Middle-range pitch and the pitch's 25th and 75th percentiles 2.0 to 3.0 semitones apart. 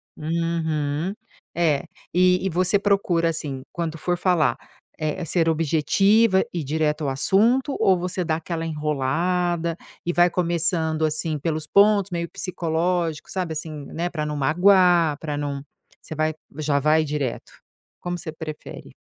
Yes: medium, 165 Hz; average, 2.7 semitones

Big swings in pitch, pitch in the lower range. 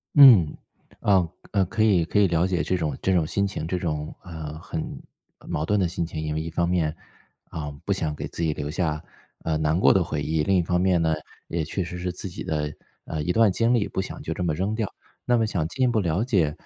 No: average, 3.6 semitones; very low, 85 Hz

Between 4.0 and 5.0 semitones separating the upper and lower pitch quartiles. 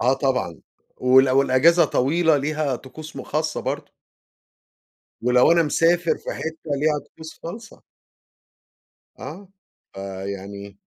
Yes: average, 4.3 semitones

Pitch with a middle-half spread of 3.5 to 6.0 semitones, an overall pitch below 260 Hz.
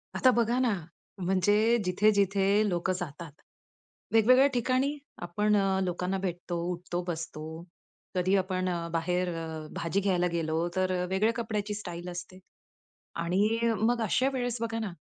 Yes: average, 3.8 semitones; high, 190 Hz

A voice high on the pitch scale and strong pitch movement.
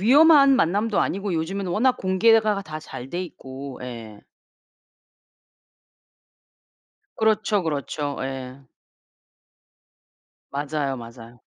No: medium, 160 Hz; wide, 7.8 semitones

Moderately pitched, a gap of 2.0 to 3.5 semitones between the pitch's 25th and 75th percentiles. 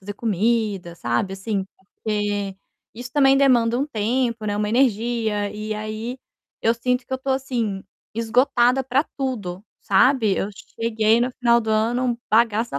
No: high, 225 Hz; average, 3.1 semitones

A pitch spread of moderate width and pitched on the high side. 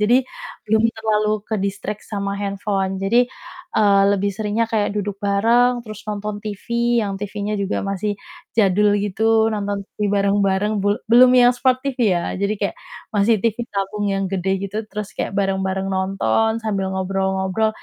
No: narrow, 1.6 semitones; high, 205 Hz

